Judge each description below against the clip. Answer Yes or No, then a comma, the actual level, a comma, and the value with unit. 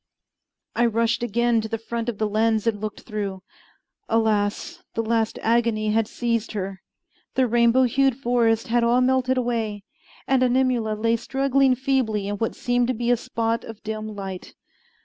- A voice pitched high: Yes, high, 230 Hz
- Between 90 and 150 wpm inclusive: No, average, 170 wpm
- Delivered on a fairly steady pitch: Yes, narrow, 2.1 semitones